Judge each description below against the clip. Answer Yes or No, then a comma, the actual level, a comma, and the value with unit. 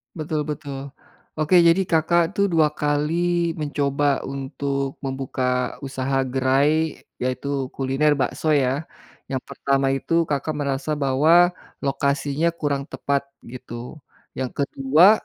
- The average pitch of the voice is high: No, medium, 140 Hz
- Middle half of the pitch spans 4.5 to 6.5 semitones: No, narrow, 2.6 semitones